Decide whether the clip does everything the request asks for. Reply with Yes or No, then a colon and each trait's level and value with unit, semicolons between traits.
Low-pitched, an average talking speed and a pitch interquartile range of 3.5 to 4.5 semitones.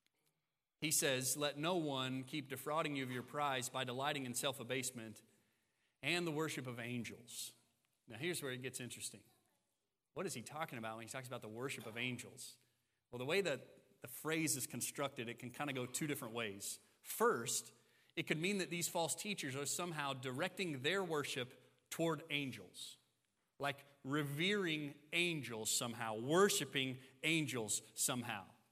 Yes: low, 130 Hz; average, 165 wpm; average, 4.1 semitones